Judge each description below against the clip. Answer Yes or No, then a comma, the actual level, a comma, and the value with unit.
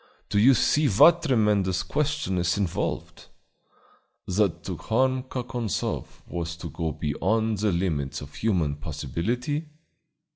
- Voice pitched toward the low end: Yes, low, 105 Hz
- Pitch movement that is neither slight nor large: No, wide, 6.7 semitones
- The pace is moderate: No, slow, 125 wpm